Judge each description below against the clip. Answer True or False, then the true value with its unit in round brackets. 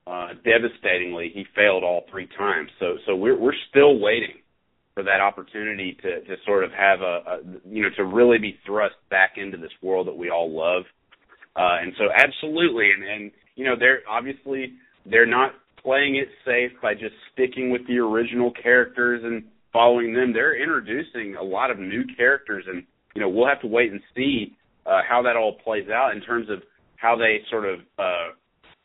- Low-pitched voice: True (115 Hz)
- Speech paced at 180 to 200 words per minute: True (190 wpm)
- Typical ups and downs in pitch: True (4.6 semitones)